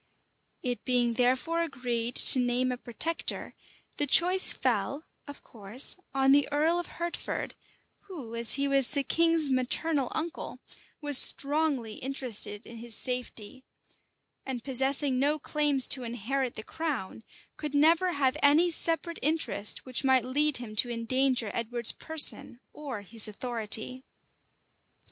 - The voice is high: Yes, very high, 265 Hz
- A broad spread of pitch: No, average, 3.7 semitones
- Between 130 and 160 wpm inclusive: Yes, slow, 135 wpm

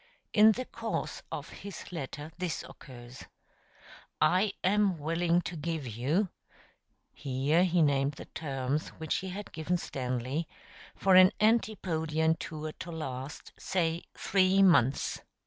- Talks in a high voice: No, medium, 160 Hz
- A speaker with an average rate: No, slow, 130 wpm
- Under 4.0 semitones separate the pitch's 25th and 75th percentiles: No, average, 4.6 semitones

